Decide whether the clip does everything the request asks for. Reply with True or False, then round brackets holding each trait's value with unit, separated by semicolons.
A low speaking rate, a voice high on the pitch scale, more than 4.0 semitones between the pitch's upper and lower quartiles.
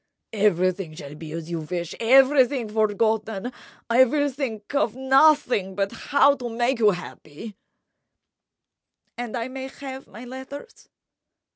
True (120 wpm; 230 Hz; 5.2 semitones)